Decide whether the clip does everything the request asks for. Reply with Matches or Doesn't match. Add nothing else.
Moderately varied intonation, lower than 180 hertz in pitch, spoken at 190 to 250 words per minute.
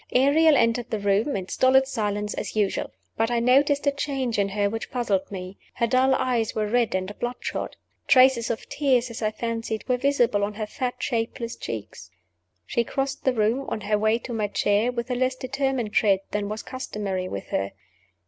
Doesn't match